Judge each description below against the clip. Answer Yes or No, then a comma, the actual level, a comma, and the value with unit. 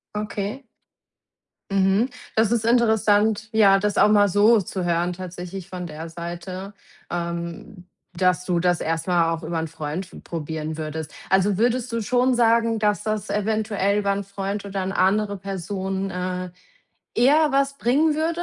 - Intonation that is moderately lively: Yes, average, 3.7 semitones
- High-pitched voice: Yes, high, 195 Hz